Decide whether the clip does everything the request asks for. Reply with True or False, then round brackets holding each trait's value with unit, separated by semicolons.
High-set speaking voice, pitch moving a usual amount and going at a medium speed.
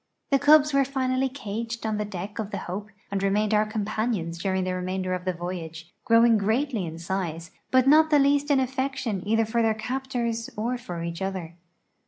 False (215 Hz; 5.7 semitones; 195 wpm)